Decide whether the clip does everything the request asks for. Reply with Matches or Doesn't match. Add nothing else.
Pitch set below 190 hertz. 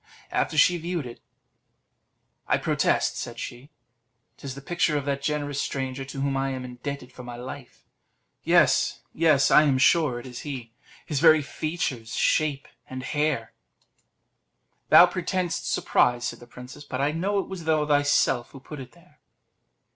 Matches